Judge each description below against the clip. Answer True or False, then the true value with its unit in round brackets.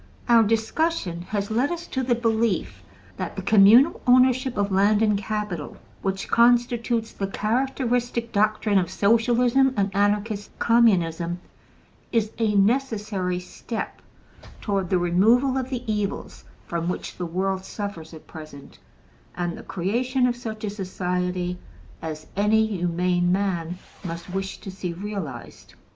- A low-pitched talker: False (205 Hz)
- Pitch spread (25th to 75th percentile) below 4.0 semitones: False (4.3 semitones)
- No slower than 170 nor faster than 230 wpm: False (135 wpm)